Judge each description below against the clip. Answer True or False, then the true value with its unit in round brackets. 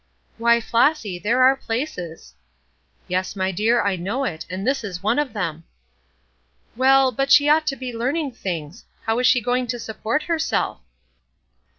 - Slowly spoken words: False (165 wpm)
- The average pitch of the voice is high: True (235 Hz)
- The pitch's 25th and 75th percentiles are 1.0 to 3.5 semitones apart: False (5.6 semitones)